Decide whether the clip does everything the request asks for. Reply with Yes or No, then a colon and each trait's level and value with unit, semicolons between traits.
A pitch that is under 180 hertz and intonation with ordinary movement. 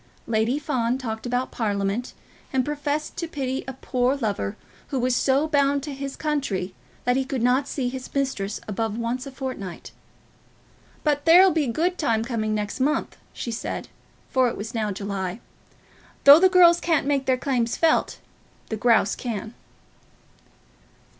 No: very high, 255 Hz; average, 4.1 semitones